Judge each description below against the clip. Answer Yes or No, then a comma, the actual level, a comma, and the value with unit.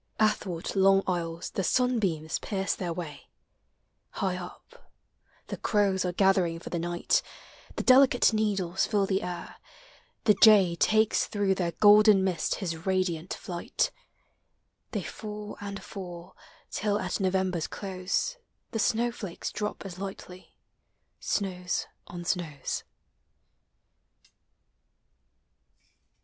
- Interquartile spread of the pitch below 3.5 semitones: Yes, average, 2.9 semitones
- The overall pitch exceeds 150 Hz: Yes, high, 190 Hz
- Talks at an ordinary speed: No, slow, 115 wpm